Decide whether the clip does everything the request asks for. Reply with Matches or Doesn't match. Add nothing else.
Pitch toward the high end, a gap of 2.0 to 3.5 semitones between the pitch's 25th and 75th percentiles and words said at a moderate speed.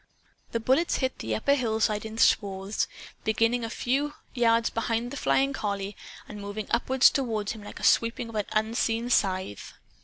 Matches